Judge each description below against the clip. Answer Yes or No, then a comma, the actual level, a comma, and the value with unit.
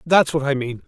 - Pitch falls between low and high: Yes, medium, 145 Hz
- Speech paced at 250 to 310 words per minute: Yes, fast, 275 wpm